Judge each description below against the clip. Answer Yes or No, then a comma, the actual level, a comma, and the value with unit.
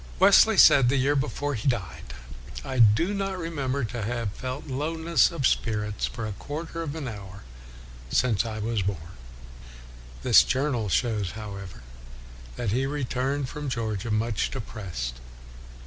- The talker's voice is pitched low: Yes, low, 120 Hz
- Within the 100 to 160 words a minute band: Yes, average, 155 wpm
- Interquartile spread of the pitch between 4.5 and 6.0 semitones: Yes, average, 5.2 semitones